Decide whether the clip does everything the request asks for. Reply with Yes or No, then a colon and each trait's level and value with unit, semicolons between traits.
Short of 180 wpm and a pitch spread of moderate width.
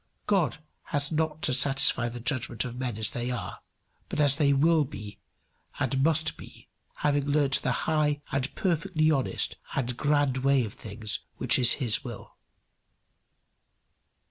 Yes: average, 150 wpm; average, 3.4 semitones